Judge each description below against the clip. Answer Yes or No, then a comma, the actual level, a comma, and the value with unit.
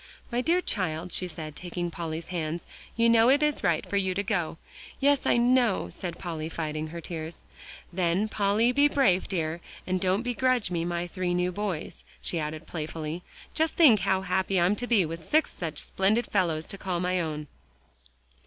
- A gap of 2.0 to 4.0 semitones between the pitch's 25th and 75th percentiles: No, average, 4.6 semitones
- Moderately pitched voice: Yes, medium, 180 Hz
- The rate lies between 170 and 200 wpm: Yes, average, 185 wpm